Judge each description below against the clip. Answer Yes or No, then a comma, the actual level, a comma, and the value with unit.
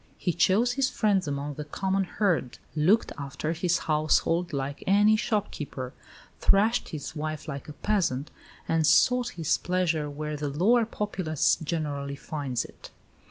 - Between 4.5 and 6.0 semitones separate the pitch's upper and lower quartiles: Yes, average, 5.0 semitones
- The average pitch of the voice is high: No, medium, 160 Hz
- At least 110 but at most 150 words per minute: Yes, average, 145 wpm